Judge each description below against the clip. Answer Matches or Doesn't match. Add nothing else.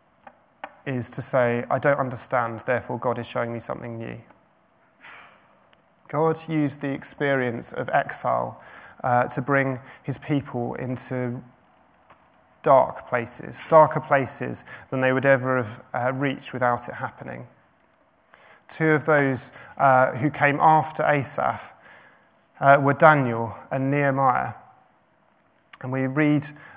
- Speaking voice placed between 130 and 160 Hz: Matches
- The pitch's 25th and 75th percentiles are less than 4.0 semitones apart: Matches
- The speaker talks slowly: Matches